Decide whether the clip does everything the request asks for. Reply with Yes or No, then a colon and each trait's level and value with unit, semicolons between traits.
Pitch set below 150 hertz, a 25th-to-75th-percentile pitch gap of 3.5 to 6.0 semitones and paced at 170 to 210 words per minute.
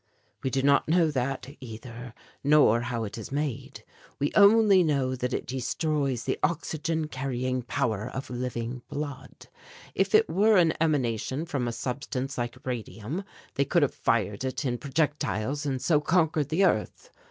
No: low, 135 Hz; average, 3.8 semitones; average, 160 wpm